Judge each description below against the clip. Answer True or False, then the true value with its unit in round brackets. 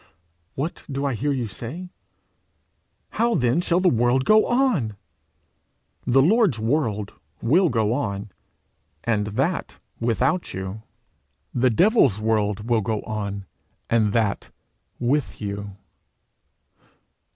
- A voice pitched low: True (120 Hz)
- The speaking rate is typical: False (115 wpm)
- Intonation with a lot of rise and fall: True (6.0 semitones)